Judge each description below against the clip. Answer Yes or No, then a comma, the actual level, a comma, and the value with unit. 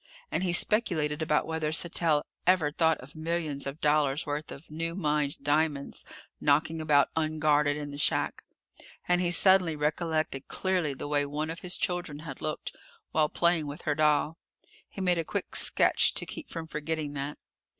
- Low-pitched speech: No, medium, 155 Hz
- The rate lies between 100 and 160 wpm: No, average, 170 wpm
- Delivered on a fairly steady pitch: Yes, narrow, 2.1 semitones